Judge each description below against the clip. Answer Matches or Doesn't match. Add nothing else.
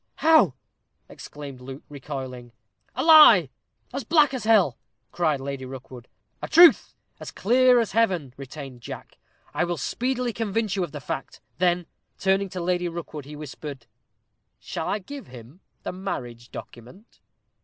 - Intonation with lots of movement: Matches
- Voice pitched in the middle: Matches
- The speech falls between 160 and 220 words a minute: Doesn't match